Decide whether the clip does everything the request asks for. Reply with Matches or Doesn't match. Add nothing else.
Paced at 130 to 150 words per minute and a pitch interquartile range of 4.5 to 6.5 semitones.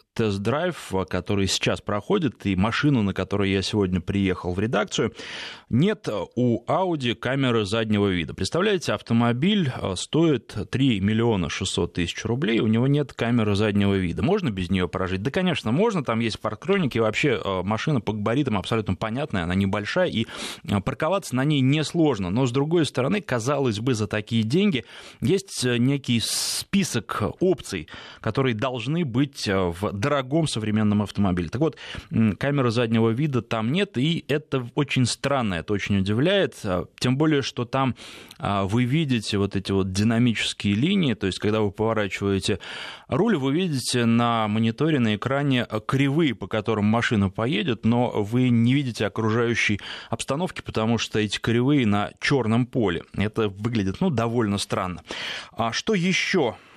Matches